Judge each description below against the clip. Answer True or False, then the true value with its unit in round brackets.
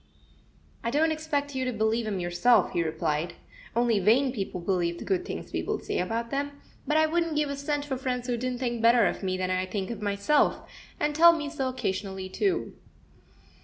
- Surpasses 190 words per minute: True (200 wpm)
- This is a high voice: True (240 Hz)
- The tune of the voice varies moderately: False (6.9 semitones)